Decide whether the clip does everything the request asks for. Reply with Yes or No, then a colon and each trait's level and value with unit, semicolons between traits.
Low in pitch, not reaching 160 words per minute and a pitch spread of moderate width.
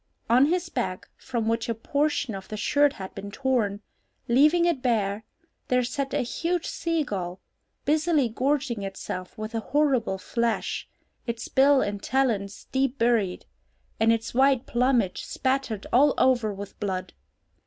No: high, 240 Hz; average, 150 wpm; average, 4.6 semitones